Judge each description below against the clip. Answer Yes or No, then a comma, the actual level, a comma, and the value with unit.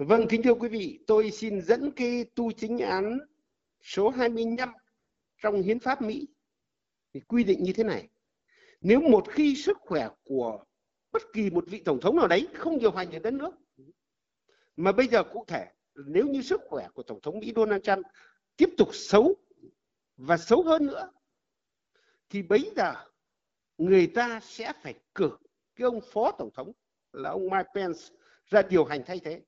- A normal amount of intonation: No, wide, 6.7 semitones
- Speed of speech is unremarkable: Yes, average, 180 wpm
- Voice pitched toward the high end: Yes, high, 230 Hz